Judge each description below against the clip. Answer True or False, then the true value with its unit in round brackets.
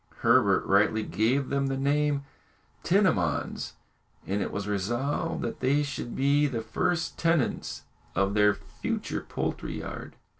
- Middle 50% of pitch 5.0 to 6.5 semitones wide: True (5.6 semitones)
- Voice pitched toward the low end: True (130 Hz)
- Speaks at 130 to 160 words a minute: True (140 wpm)